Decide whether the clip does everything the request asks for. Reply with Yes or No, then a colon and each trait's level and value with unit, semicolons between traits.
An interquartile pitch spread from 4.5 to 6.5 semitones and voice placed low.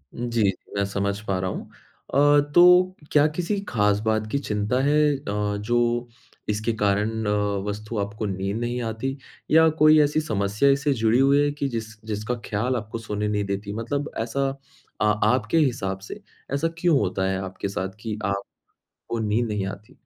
Yes: average, 5.1 semitones; low, 110 Hz